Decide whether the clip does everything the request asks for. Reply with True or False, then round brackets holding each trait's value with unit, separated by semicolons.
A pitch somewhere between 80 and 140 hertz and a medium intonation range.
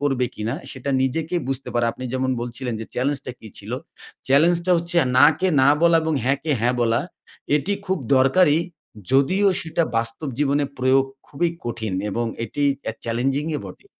True (135 Hz; 4.5 semitones)